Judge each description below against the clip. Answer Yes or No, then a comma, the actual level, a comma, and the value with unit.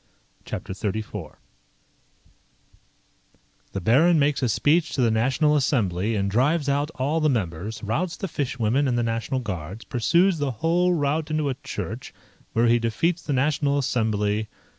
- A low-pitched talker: Yes, low, 130 Hz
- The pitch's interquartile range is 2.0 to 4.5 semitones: No, wide, 5.5 semitones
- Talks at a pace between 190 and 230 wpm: No, average, 155 wpm